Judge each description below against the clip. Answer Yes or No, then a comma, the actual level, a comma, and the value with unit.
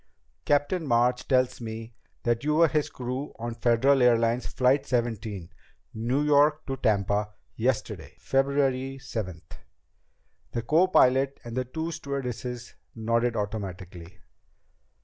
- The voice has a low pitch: Yes, low, 125 Hz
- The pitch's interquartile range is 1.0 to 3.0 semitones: No, average, 3.4 semitones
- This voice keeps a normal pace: No, slow, 115 wpm